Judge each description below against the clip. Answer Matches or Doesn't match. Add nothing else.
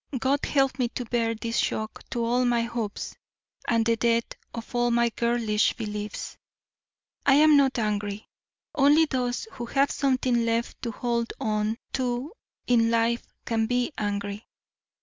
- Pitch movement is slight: Matches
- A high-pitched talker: Matches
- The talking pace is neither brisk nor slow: Matches